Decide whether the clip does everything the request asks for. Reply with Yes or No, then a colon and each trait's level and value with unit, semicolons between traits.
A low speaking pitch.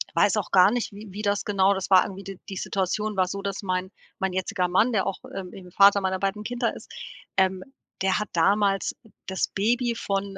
No: high, 195 Hz